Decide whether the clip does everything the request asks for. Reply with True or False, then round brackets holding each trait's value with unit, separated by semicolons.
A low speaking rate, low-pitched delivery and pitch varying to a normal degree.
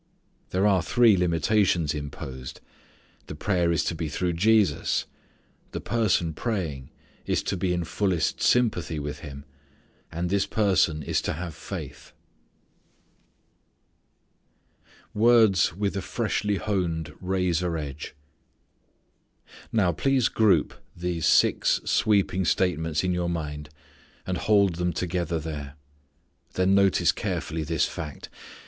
True (120 wpm; 90 Hz; 3.8 semitones)